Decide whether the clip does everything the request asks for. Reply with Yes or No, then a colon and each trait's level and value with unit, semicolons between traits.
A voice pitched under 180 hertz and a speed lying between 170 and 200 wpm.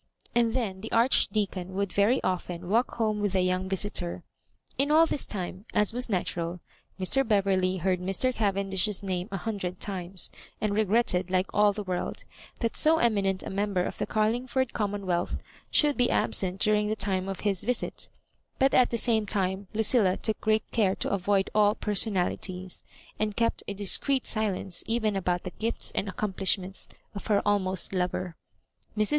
No: high, 200 Hz; average, 175 wpm